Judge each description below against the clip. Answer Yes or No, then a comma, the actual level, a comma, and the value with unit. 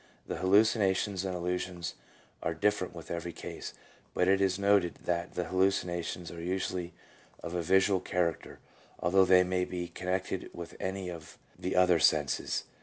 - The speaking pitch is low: Yes, very low, 90 Hz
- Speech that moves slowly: No, average, 155 wpm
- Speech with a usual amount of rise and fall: No, narrow, 1.6 semitones